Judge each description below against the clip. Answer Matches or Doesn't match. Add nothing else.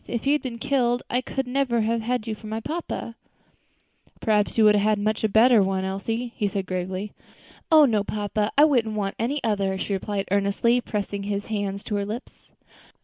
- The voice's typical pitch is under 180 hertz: Doesn't match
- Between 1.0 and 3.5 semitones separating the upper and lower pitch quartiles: Matches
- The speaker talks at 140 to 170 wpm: Doesn't match